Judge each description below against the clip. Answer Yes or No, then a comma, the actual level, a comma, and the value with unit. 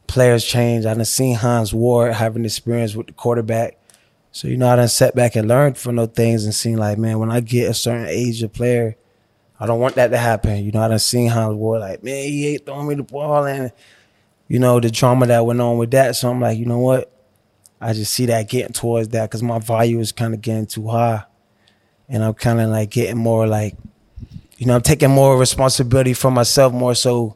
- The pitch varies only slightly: Yes, narrow, 1.8 semitones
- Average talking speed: No, fast, 235 wpm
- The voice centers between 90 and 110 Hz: No, low, 120 Hz